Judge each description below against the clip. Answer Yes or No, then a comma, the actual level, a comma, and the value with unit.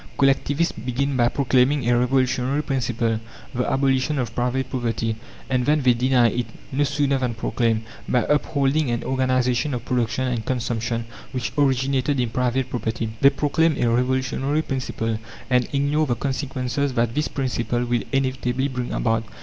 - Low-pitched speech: Yes, low, 130 Hz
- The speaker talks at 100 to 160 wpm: Yes, average, 155 wpm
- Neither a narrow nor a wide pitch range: No, narrow, 2.2 semitones